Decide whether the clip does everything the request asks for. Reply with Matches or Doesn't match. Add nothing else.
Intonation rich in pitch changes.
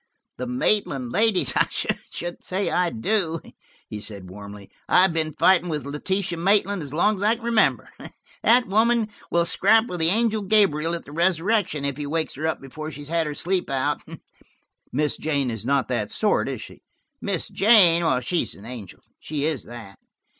Matches